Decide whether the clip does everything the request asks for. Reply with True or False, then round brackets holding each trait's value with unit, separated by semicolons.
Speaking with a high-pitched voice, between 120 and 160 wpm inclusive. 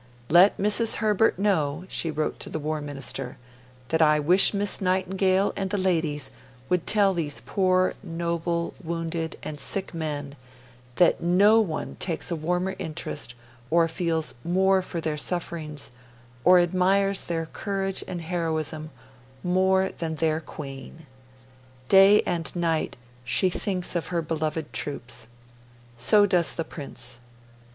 False (170 Hz; 135 wpm)